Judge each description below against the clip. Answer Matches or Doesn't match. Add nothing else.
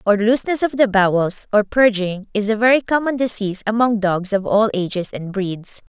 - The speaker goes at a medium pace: Matches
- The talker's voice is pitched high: Matches